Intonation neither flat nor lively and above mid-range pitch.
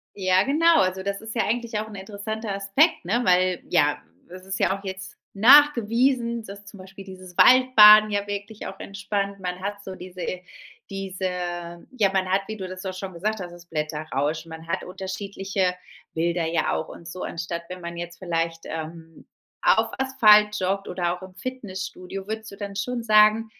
Yes: average, 3.0 semitones; high, 195 Hz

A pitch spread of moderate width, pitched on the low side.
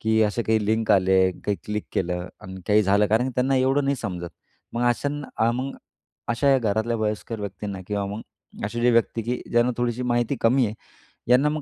Yes: average, 3.3 semitones; low, 115 Hz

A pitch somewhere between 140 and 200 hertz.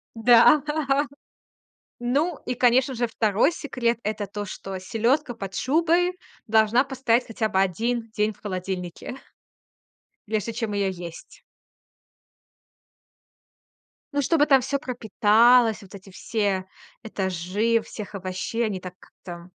No: high, 225 Hz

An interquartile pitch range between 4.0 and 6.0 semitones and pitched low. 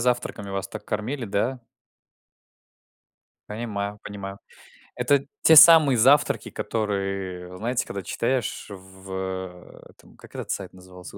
Yes: average, 4.5 semitones; low, 100 Hz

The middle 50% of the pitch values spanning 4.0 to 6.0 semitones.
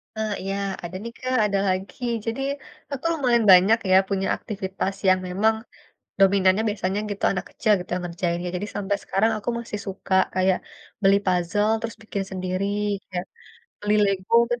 No: narrow, 2.6 semitones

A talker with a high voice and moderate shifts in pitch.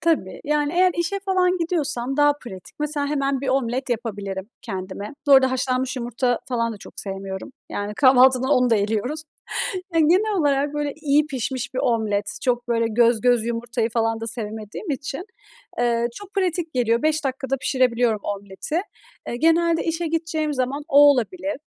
Yes: very high, 260 Hz; average, 4.6 semitones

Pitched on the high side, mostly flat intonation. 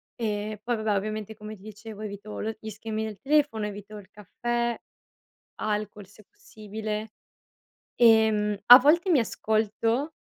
Yes: high, 215 Hz; narrow, 1.6 semitones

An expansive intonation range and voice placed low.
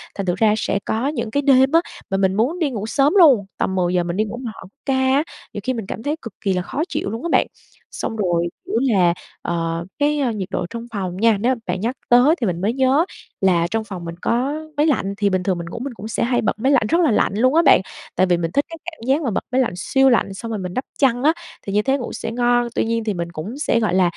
No: wide, 5.7 semitones; high, 225 Hz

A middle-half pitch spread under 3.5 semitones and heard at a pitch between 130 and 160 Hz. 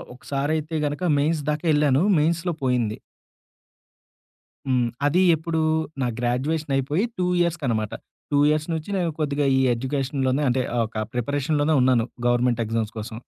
No: average, 3.9 semitones; medium, 140 Hz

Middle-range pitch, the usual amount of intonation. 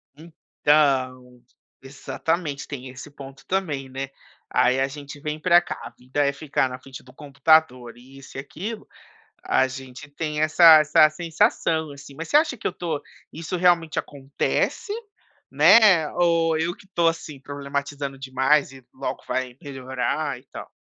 Yes: medium, 145 Hz; average, 3.2 semitones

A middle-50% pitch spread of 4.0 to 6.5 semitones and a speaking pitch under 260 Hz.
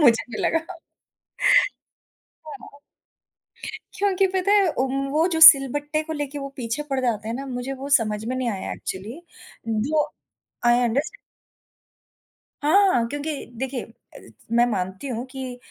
No: average, 4.5 semitones; very high, 270 Hz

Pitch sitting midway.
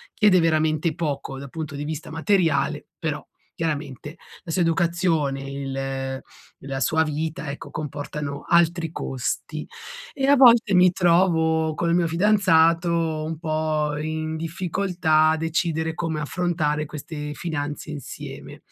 Yes: medium, 160 Hz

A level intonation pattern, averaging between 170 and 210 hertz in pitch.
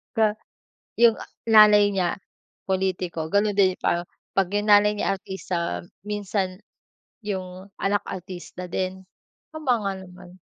Yes: narrow, 2.1 semitones; high, 190 Hz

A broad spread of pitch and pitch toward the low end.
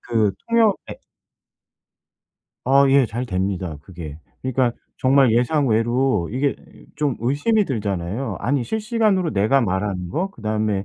Yes: wide, 5.7 semitones; low, 120 Hz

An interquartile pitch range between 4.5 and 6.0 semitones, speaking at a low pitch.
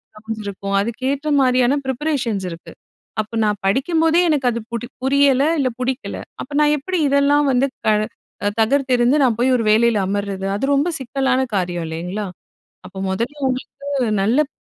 No: average, 4.8 semitones; very high, 250 Hz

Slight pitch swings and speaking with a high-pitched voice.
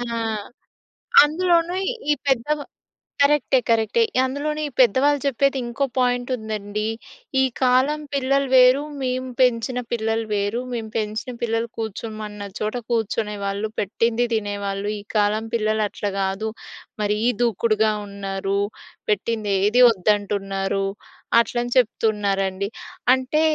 No: average, 3.7 semitones; high, 225 Hz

